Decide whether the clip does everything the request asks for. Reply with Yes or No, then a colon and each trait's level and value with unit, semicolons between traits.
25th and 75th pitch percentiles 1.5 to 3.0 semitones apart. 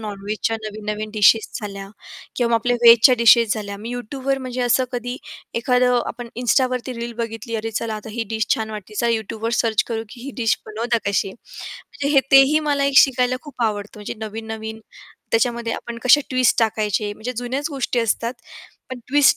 Yes: narrow, 2.5 semitones